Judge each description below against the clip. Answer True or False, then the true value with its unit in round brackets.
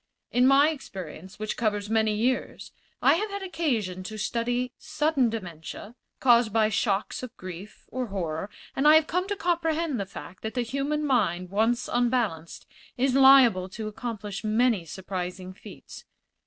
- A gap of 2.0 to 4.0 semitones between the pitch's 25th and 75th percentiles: False (5.4 semitones)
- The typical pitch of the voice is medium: False (225 Hz)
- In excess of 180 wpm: False (155 wpm)